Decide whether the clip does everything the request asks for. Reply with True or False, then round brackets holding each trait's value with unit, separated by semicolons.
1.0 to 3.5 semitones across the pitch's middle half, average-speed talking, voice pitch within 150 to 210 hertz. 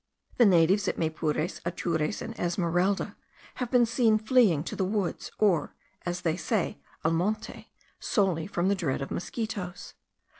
False (4.3 semitones; 150 wpm; 185 Hz)